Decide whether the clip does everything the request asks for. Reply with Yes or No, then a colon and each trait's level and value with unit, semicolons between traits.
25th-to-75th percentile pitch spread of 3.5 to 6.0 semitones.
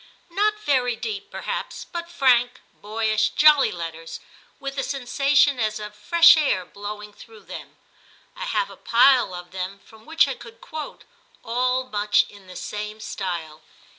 Yes: average, 5.2 semitones